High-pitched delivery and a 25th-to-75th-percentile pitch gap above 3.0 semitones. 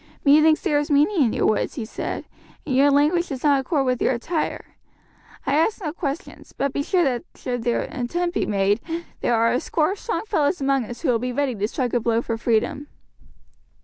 Yes: very high, 275 Hz; average, 4.2 semitones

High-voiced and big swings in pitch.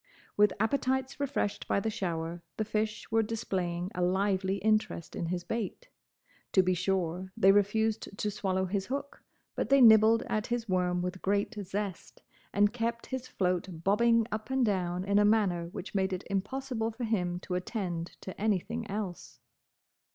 No: high, 205 Hz; average, 3.3 semitones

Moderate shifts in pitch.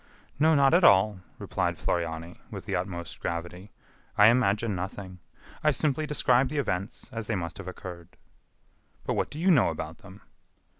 No: wide, 6.7 semitones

